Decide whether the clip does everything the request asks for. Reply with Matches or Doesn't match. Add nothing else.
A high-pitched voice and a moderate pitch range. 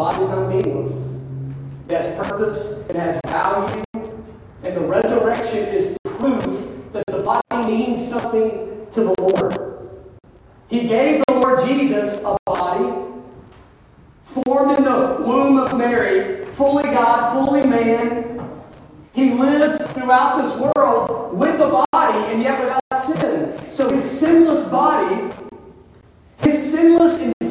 Matches